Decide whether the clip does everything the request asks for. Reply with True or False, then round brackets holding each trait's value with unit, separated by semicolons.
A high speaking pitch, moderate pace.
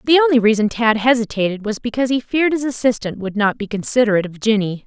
False (230 Hz; 210 wpm)